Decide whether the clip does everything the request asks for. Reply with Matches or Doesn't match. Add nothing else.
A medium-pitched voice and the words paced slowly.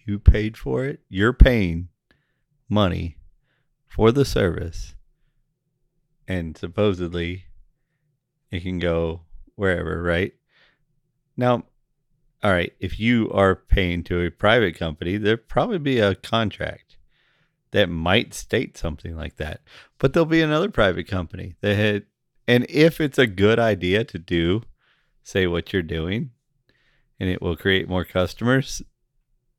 Doesn't match